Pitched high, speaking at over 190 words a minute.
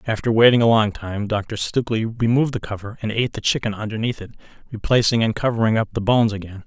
No: low, 110 Hz; fast, 205 wpm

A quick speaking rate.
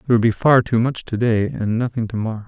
Yes: fast, 245 wpm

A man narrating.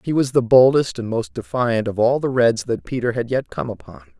Yes: male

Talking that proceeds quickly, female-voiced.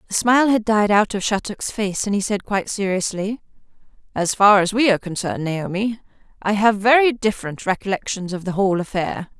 No: average, 185 wpm; female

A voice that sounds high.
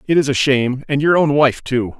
No: low, 135 Hz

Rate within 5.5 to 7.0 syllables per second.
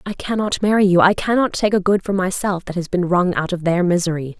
Yes: 5.9 syllables/s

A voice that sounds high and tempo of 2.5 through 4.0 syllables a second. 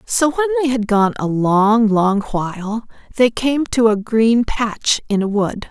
Yes: high, 225 Hz; 3.9 syllables/s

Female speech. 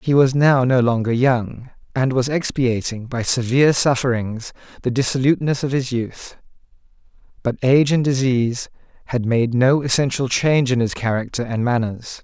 No: male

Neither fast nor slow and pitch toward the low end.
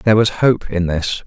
No: fast, 235 wpm; low, 100 Hz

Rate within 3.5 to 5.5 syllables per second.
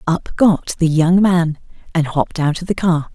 Yes: 4.6 syllables/s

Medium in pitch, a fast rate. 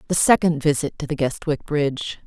No: medium, 150 Hz; average, 185 wpm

